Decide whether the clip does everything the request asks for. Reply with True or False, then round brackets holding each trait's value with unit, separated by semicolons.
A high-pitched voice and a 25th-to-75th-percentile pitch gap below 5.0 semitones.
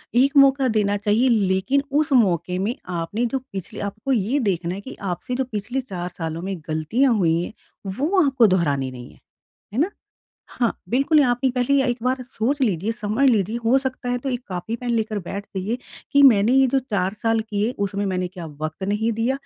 False (225 Hz; 5.4 semitones)